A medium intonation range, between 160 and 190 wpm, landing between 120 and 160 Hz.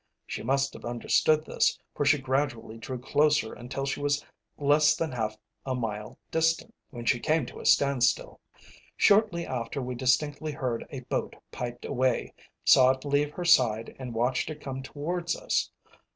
Yes: average, 3.5 semitones; average, 165 wpm; low, 135 Hz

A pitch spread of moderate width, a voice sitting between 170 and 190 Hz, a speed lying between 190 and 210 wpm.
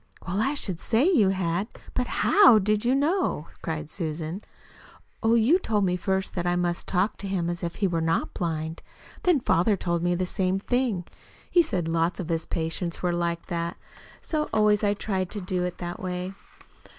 Yes: average, 3.9 semitones; medium, 185 Hz; average, 200 wpm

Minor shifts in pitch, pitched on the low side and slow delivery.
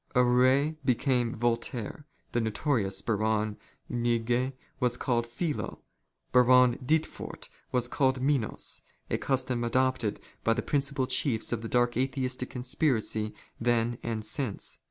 Yes: narrow, 2.2 semitones; low, 125 Hz; slow, 115 wpm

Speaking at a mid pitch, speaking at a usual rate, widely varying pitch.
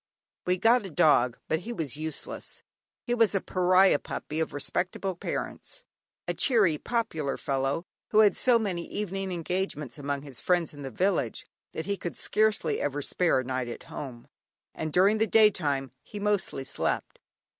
Yes: medium, 175 Hz; average, 170 wpm; wide, 6.0 semitones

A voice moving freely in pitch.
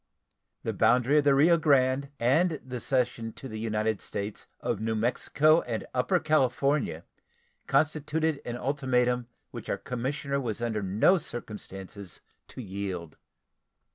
No: average, 4.3 semitones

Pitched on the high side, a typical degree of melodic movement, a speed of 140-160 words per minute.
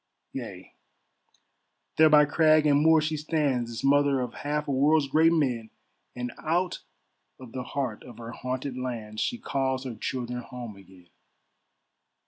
No: low, 135 Hz; average, 3.7 semitones; average, 150 wpm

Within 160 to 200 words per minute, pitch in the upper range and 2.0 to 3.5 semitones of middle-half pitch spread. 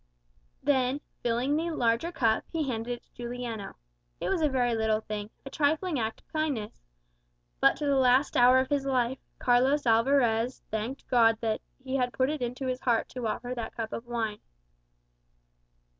Yes: average, 175 wpm; high, 245 Hz; average, 2.9 semitones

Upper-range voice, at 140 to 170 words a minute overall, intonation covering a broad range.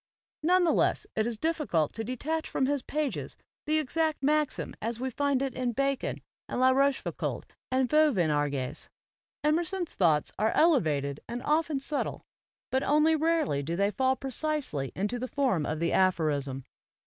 Yes: very high, 260 Hz; average, 160 wpm; wide, 8.5 semitones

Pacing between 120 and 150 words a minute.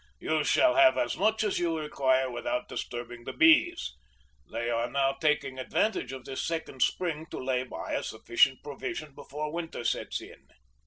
No: average, 170 wpm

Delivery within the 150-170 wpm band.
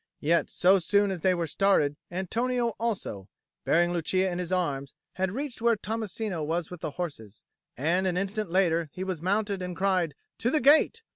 No: average, 185 wpm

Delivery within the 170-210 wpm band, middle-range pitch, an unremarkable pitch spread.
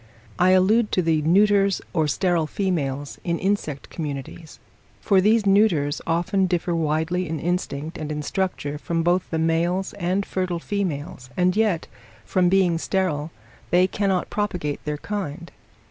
No: average, 145 wpm; medium, 175 Hz; average, 3.5 semitones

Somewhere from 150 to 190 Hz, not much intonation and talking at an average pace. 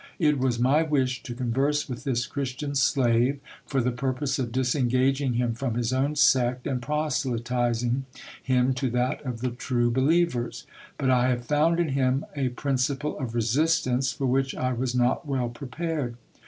No: low, 130 Hz; narrow, 2.2 semitones; average, 170 wpm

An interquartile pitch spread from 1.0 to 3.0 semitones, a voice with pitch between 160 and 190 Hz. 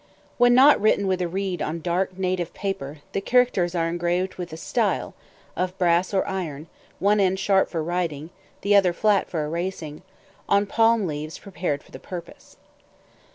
Yes: average, 2.7 semitones; medium, 185 Hz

